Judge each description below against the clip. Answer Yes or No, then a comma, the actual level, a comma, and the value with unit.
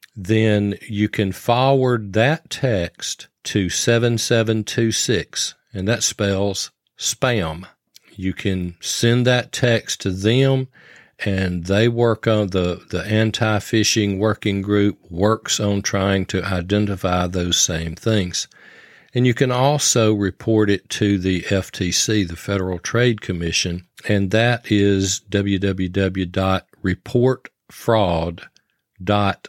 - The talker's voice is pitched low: Yes, low, 105 Hz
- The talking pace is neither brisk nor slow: No, slow, 110 wpm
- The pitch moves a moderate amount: Yes, average, 3.4 semitones